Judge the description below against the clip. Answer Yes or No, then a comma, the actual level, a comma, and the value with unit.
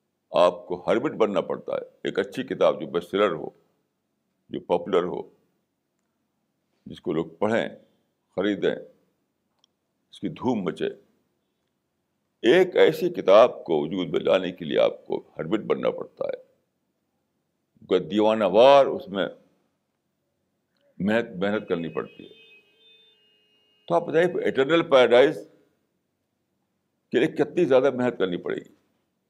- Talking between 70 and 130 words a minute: Yes, average, 125 wpm